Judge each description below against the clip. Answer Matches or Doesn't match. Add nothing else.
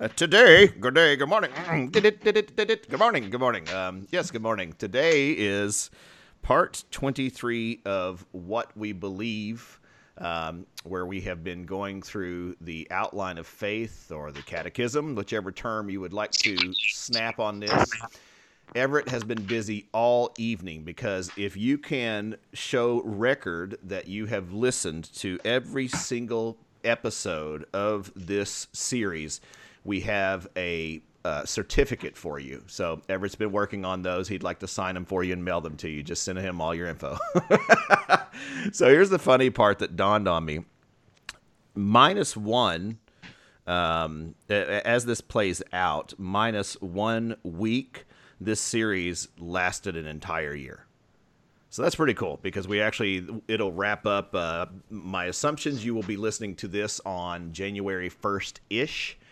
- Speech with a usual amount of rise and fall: Matches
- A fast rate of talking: Doesn't match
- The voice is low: Matches